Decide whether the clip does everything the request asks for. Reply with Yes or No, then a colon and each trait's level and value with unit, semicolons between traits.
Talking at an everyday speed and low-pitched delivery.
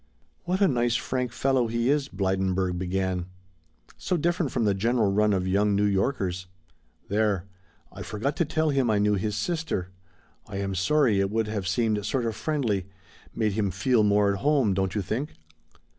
Yes: average, 180 wpm; low, 105 Hz